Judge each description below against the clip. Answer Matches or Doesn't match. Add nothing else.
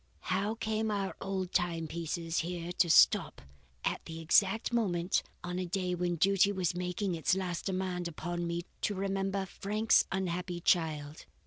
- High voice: Doesn't match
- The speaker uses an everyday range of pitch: Doesn't match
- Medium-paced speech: Matches